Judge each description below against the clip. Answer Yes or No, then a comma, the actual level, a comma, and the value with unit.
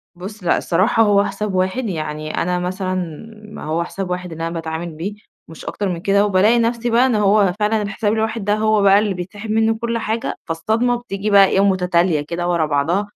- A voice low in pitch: No, high, 195 Hz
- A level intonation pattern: No, average, 3.7 semitones